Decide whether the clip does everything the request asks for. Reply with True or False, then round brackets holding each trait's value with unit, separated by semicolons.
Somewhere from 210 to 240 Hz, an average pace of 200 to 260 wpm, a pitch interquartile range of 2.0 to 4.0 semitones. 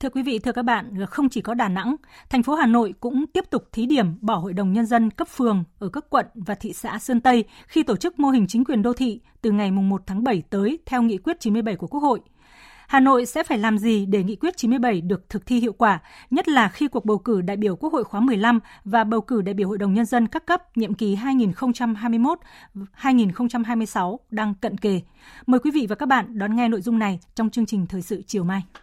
True (230 Hz; 250 wpm; 3.5 semitones)